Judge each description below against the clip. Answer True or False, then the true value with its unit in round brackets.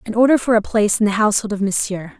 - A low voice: False (210 Hz)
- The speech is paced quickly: True (275 wpm)